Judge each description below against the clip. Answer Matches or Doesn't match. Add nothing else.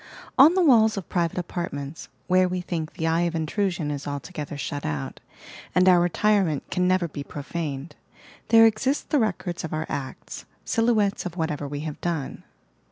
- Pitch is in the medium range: Matches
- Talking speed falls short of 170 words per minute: Doesn't match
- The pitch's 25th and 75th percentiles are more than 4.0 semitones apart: Matches